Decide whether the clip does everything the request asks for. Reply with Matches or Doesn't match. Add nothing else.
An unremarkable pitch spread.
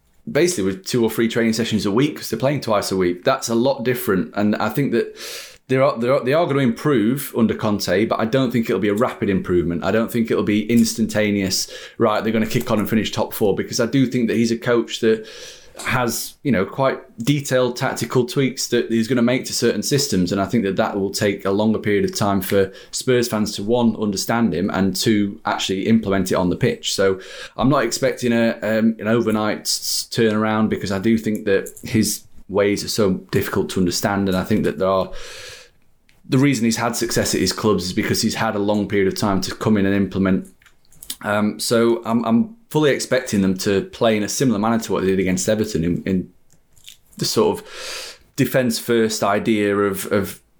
Matches